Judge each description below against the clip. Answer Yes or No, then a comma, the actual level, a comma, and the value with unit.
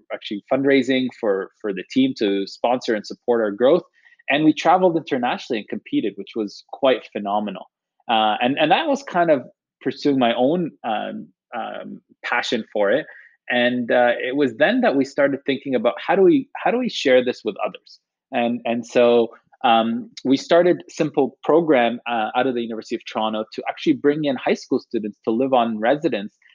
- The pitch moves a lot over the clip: No, average, 3.2 semitones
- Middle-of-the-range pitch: No, low, 125 Hz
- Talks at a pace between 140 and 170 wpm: No, average, 190 wpm